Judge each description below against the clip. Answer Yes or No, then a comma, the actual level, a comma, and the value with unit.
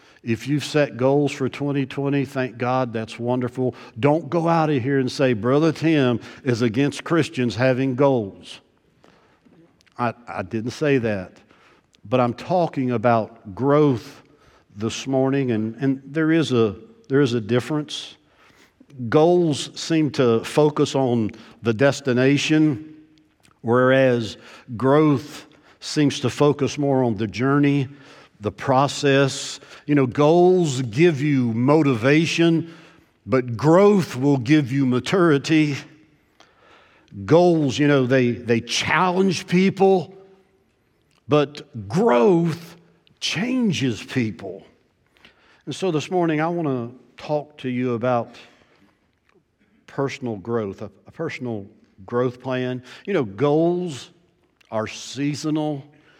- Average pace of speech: No, slow, 115 wpm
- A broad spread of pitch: No, average, 4.0 semitones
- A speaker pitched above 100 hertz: Yes, low, 135 Hz